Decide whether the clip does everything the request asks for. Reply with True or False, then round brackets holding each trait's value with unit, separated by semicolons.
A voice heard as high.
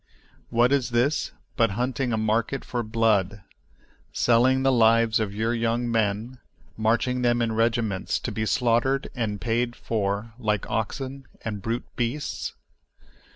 False (115 Hz)